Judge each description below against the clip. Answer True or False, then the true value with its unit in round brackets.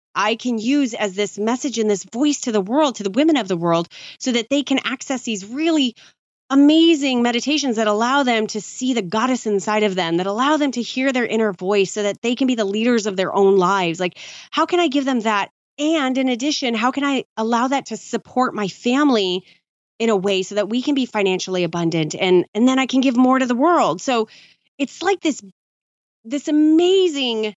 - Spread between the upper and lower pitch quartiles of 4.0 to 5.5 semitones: True (5.0 semitones)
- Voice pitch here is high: True (240 Hz)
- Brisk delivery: True (220 wpm)